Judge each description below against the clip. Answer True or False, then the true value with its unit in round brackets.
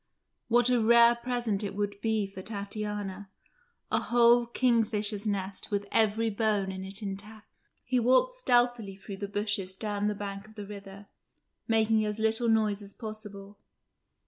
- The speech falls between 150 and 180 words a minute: True (155 wpm)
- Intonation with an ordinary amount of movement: False (2.2 semitones)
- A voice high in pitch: True (210 Hz)